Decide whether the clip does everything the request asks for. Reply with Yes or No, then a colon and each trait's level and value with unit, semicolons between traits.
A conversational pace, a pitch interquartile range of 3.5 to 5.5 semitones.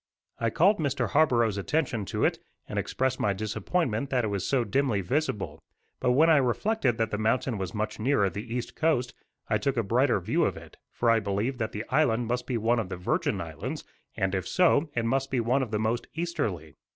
No: fast, 215 wpm; average, 4.4 semitones